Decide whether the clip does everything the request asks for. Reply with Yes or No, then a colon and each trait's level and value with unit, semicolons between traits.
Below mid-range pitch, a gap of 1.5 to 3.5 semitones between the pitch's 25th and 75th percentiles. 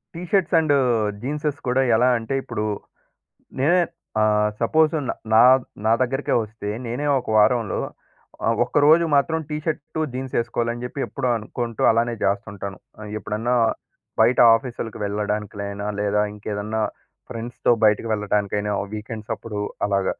No: low, 115 Hz; average, 4.0 semitones